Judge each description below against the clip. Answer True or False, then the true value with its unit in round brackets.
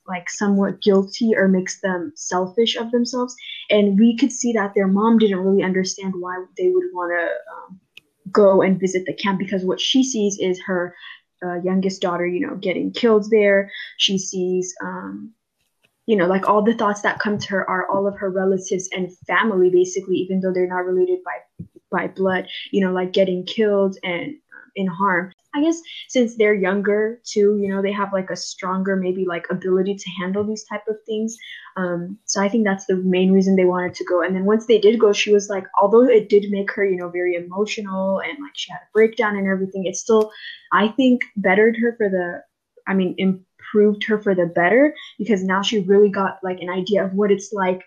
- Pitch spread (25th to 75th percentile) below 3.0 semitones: True (2.6 semitones)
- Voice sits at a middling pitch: False (195 Hz)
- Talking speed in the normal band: False (210 wpm)